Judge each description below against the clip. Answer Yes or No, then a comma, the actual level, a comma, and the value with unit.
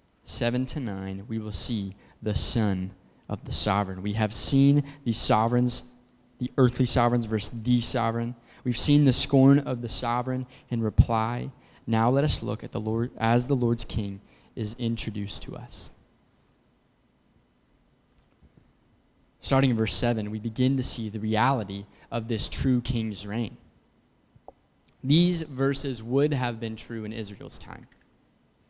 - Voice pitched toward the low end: Yes, low, 120 Hz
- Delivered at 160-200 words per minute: No, average, 145 wpm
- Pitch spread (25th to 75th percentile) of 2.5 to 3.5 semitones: Yes, average, 2.8 semitones